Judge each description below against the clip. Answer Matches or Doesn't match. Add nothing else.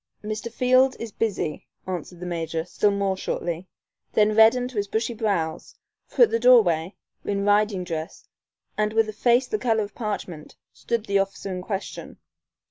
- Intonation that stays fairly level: Doesn't match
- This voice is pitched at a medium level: Doesn't match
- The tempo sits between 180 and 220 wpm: Doesn't match